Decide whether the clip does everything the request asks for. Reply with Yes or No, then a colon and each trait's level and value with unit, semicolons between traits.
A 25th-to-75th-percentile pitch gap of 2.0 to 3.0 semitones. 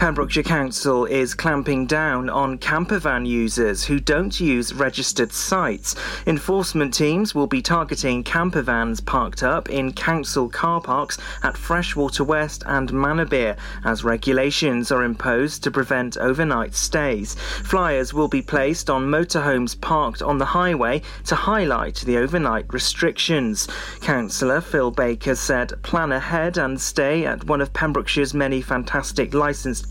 No: average, 3.5 semitones